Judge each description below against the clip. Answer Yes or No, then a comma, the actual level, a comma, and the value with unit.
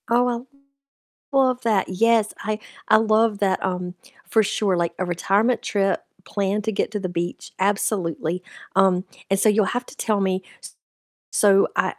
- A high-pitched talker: Yes, high, 200 Hz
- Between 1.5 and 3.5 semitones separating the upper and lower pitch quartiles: Yes, average, 2.8 semitones